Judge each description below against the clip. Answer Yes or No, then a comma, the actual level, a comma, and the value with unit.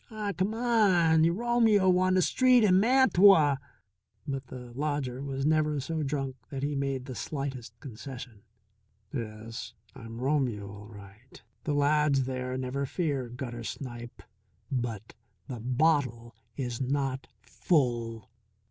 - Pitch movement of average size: Yes, average, 4.9 semitones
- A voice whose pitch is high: No, low, 135 Hz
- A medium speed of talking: No, slow, 130 wpm